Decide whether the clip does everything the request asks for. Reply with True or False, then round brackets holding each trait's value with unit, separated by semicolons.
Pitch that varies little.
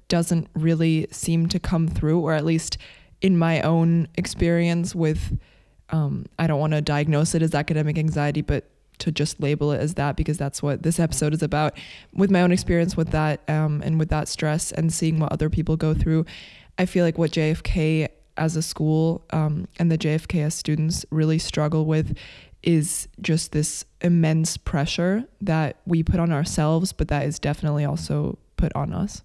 True (1.6 semitones)